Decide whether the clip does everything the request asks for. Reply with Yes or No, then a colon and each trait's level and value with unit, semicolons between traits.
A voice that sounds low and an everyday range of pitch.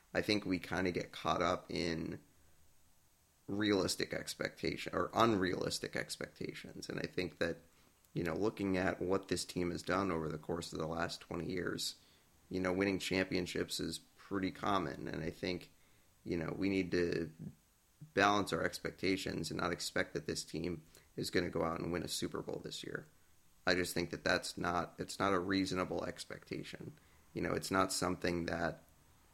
No: very low, 90 Hz; narrow, 2.2 semitones